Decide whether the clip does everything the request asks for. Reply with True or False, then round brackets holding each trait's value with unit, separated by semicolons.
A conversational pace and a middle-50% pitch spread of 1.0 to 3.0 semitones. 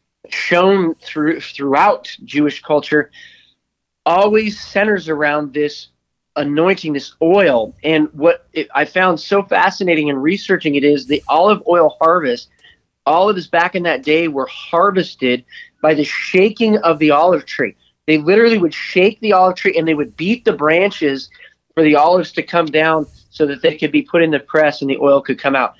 False (180 wpm; 4.2 semitones)